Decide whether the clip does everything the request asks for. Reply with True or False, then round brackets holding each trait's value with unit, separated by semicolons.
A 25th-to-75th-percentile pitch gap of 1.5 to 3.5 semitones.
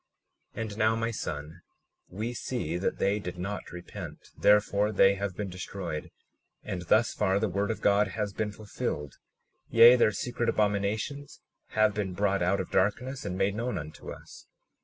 True (2.5 semitones)